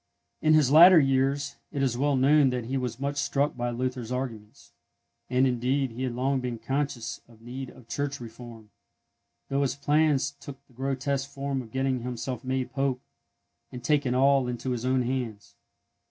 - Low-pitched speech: Yes, low, 130 Hz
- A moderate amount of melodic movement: No, narrow, 2.2 semitones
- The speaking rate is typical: Yes, average, 175 wpm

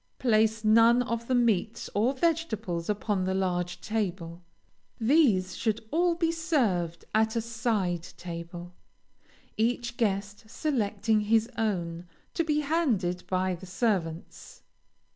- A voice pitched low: No, high, 215 Hz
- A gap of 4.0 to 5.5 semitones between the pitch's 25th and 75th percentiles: Yes, average, 4.6 semitones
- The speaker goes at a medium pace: No, slow, 125 wpm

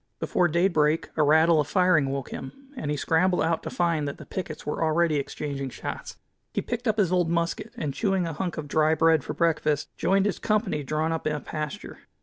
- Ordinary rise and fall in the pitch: Yes, average, 3.2 semitones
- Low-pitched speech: No, medium, 160 Hz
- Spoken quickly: Yes, fast, 215 wpm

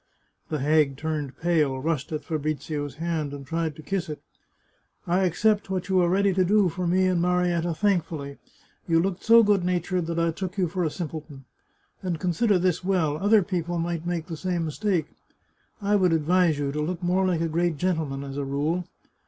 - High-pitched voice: No, medium, 170 Hz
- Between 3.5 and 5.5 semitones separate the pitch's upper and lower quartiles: No, average, 3.0 semitones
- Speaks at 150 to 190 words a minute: No, average, 200 wpm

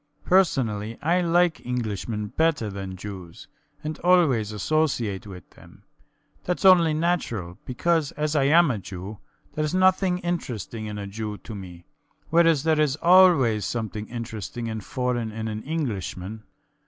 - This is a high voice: No, low, 120 Hz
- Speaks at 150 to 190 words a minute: No, average, 140 wpm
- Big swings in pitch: Yes, wide, 7.6 semitones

